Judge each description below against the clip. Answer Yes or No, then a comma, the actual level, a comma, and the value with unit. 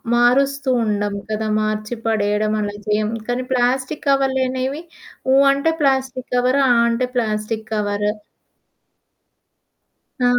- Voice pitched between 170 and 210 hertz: No, high, 245 Hz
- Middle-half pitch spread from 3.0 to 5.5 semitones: Yes, average, 3.7 semitones